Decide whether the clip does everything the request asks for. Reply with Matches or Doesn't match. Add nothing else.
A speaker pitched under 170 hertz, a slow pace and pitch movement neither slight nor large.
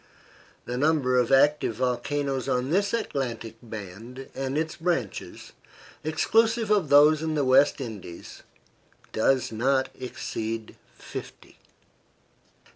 Matches